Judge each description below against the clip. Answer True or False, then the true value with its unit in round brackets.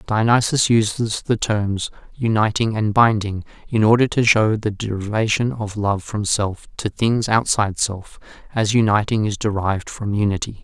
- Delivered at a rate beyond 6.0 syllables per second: False (4.6 syllables/s)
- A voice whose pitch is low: True (110 Hz)